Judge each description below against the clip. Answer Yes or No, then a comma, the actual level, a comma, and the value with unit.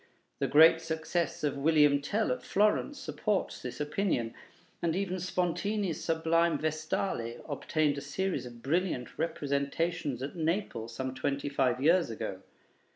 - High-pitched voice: No, medium, 160 Hz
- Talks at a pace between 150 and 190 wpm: No, slow, 135 wpm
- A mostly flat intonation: No, average, 4.0 semitones